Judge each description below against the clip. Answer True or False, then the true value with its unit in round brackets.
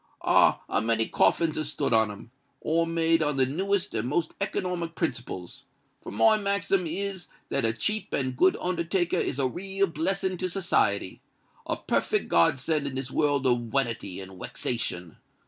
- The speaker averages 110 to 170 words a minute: True (165 wpm)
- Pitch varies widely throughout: True (7.1 semitones)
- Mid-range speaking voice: True (150 Hz)